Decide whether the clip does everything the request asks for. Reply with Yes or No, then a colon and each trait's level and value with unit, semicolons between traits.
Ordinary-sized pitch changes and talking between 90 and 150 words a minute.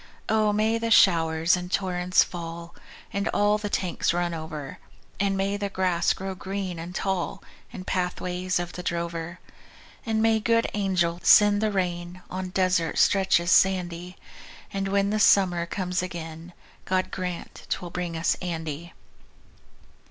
No: narrow, 2.3 semitones; average, 145 wpm